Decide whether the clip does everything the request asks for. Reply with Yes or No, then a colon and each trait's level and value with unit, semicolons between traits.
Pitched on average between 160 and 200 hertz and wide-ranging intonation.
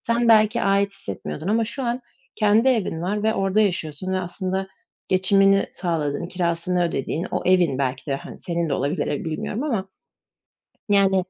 No: high, 190 Hz; average, 3.7 semitones